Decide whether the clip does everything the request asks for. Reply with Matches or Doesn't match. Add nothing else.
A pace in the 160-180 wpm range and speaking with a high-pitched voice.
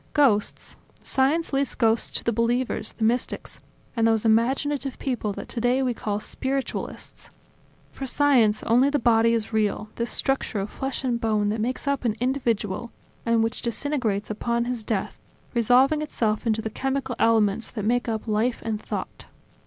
Matches